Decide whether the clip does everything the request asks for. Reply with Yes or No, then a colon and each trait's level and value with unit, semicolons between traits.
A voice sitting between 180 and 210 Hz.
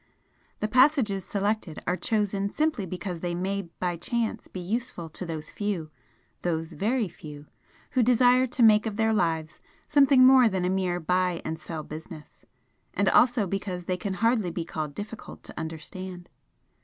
Yes: high, 190 Hz